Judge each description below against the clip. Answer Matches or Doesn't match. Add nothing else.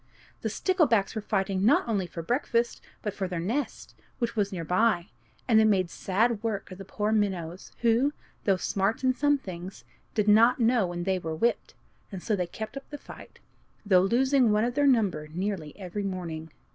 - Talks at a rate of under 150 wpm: Doesn't match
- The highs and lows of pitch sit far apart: Doesn't match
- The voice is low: Doesn't match